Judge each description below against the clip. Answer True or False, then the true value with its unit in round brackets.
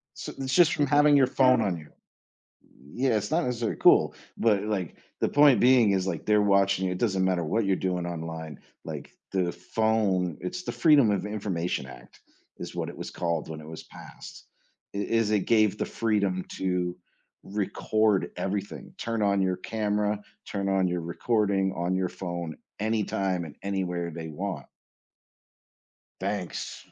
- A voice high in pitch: False (100 Hz)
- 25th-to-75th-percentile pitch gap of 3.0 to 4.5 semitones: True (3.5 semitones)